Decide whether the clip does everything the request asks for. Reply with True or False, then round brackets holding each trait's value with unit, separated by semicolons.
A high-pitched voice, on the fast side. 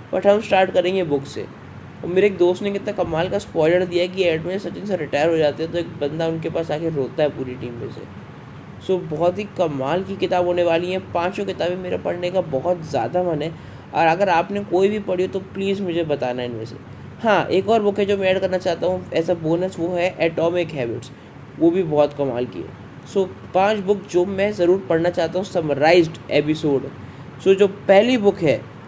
False (175 Hz; 220 wpm)